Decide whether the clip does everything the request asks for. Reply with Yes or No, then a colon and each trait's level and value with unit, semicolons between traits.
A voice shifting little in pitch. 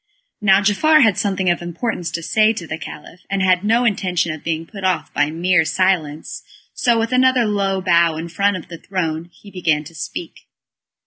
No: average, 3.8 semitones